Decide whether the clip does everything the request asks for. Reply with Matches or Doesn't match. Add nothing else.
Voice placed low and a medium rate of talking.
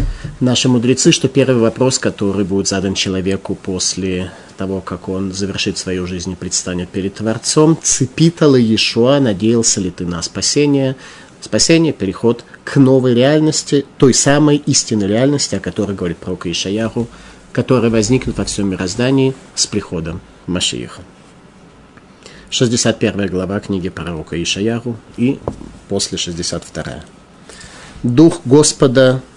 Matches